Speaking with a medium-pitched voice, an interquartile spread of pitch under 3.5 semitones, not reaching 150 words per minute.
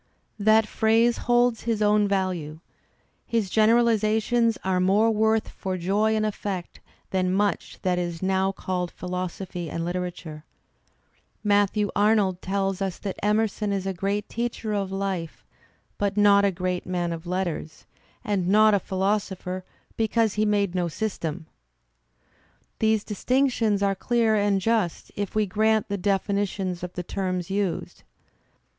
No: high, 200 Hz; average, 2.8 semitones; average, 140 wpm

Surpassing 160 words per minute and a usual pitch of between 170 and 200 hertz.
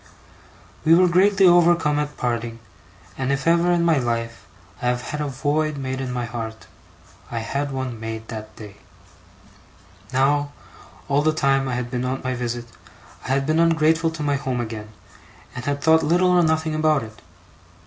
No: average, 180 wpm; medium, 140 Hz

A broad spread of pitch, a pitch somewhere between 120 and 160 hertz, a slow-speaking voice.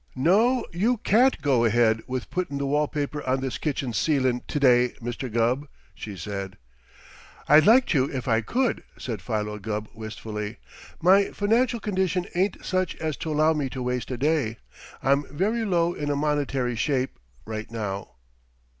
No: wide, 6.7 semitones; medium, 140 Hz; average, 165 wpm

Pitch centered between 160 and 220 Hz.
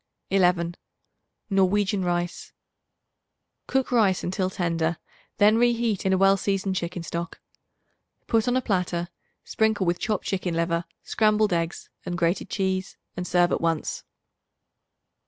Yes: medium, 185 Hz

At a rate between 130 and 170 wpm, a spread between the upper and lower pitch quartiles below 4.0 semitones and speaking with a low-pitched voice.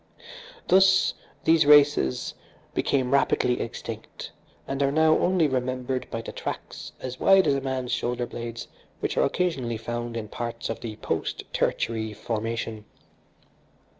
Yes: slow, 135 wpm; average, 3.6 semitones; low, 125 Hz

